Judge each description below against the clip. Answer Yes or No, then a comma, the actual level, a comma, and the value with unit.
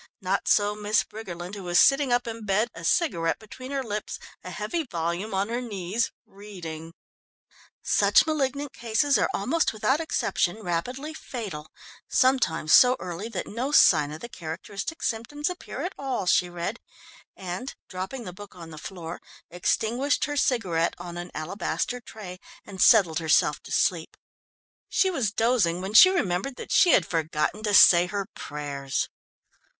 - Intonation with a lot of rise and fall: Yes, wide, 6.2 semitones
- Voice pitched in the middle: No, high, 205 Hz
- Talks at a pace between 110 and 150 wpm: No, average, 160 wpm